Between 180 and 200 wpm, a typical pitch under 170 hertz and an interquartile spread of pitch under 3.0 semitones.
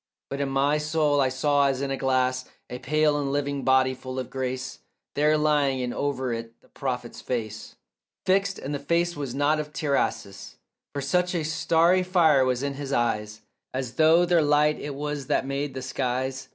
Yes: average, 190 wpm; medium, 140 Hz; narrow, 2.6 semitones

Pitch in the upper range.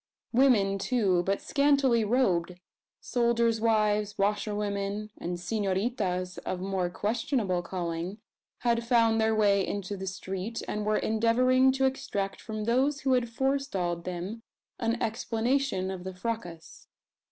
Yes: high, 215 Hz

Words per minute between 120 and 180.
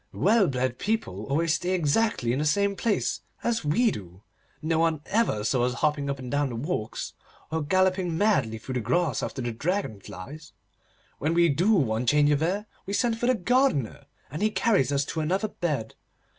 No: average, 190 wpm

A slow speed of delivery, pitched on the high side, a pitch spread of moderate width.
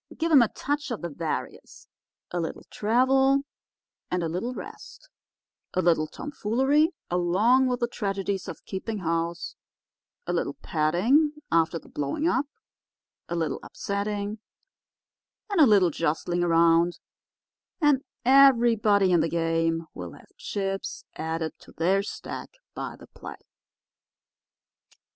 No: slow, 125 wpm; high, 195 Hz; wide, 7.1 semitones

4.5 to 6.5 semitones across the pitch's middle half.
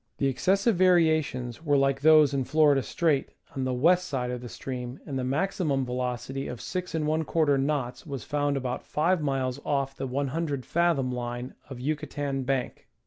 No: average, 3.4 semitones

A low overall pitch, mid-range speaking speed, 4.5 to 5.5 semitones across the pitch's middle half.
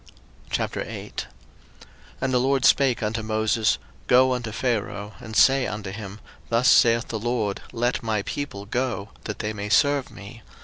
No: low, 115 Hz; average, 150 wpm; average, 3.1 semitones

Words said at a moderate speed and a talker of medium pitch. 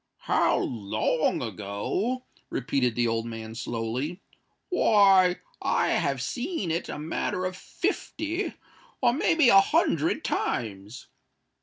No: slow, 115 wpm; medium, 155 Hz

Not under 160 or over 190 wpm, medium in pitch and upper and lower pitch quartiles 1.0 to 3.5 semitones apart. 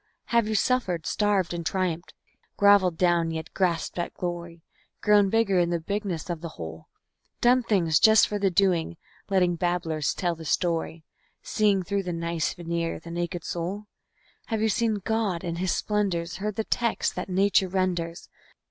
Yes: average, 165 wpm; medium, 180 Hz; average, 3.2 semitones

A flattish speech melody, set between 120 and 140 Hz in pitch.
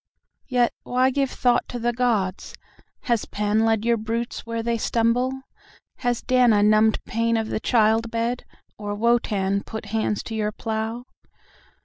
No: narrow, 1.8 semitones; high, 230 Hz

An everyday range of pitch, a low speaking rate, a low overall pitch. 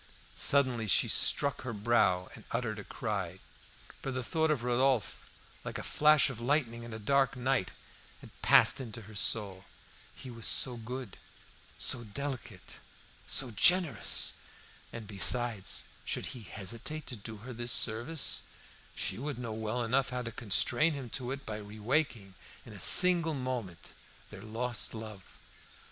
No: average, 3.6 semitones; average, 155 wpm; low, 120 Hz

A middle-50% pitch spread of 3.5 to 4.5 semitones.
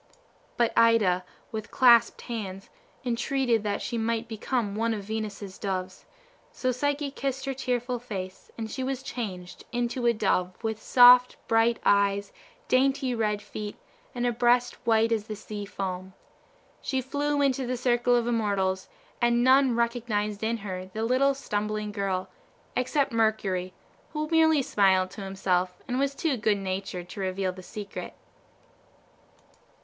Yes: average, 3.9 semitones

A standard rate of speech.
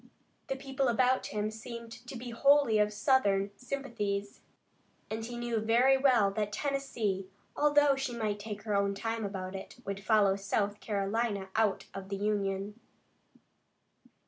Yes: average, 145 wpm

